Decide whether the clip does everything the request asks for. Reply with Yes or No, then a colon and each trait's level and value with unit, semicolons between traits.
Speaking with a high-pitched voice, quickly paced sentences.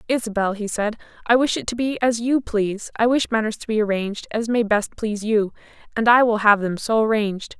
Yes: high, 220 Hz; fast, 230 wpm